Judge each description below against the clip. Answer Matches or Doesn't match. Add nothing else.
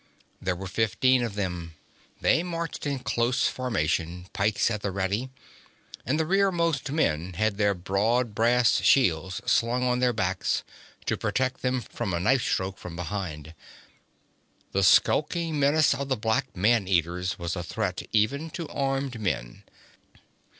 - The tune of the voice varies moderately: Doesn't match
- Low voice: Matches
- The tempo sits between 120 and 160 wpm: Matches